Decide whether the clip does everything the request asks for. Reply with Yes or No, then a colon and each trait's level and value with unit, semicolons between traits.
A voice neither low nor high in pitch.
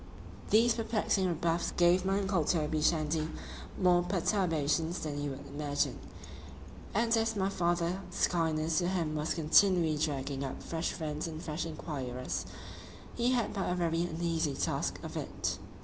Yes: medium, 165 Hz